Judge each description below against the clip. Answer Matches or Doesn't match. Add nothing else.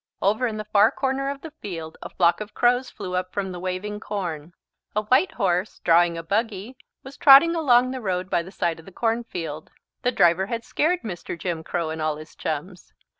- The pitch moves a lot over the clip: Matches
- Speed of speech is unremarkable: Doesn't match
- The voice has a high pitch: Matches